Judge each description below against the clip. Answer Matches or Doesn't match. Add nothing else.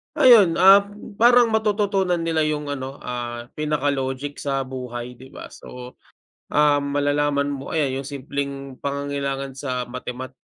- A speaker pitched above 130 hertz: Matches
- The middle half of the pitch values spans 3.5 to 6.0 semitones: Doesn't match